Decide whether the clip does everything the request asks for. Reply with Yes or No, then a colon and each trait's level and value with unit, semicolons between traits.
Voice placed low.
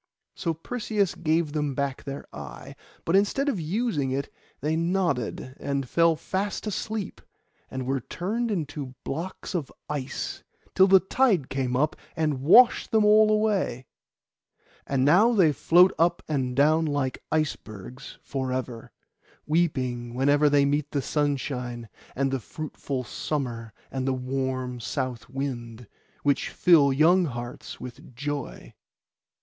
No: medium, 145 Hz